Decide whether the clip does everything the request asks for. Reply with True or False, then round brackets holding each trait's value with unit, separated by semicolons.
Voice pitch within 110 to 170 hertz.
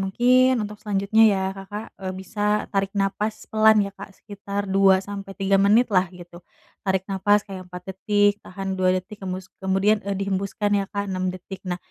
False (195 Hz)